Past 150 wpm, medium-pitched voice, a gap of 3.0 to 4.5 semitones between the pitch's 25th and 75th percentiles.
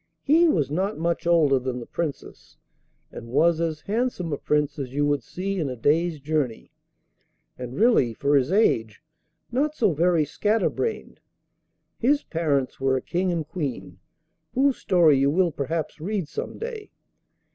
No: average, 160 wpm; medium, 160 Hz; wide, 5.5 semitones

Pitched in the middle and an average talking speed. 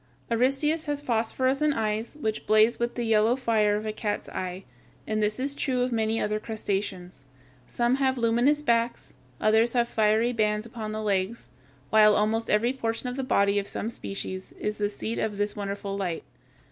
No: high, 220 Hz; average, 180 wpm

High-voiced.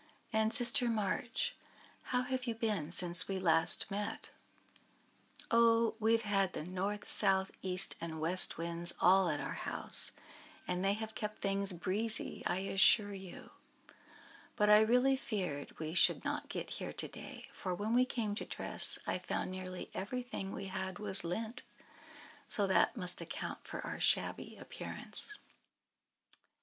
Yes: high, 200 Hz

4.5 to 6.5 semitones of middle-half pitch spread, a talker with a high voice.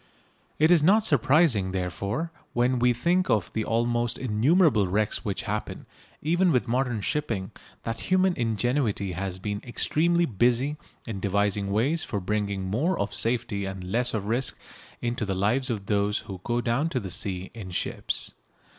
No: average, 5.1 semitones; low, 115 Hz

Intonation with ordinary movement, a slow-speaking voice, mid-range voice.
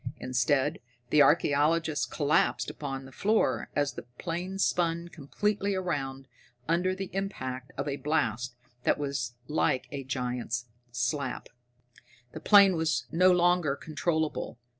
Yes: average, 4.7 semitones; slow, 125 wpm; medium, 150 Hz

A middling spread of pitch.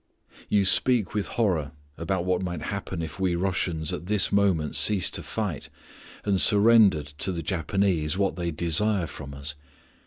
Yes: average, 3.7 semitones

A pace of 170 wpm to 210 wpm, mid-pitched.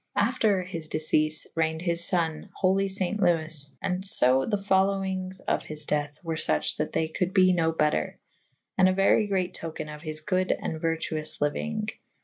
Yes: average, 185 wpm; medium, 175 Hz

